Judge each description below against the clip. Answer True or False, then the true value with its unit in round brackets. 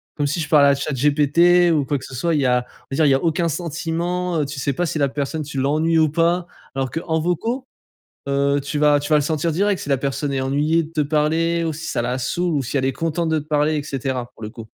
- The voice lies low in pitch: False (150 Hz)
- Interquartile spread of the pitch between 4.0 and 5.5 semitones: False (3.0 semitones)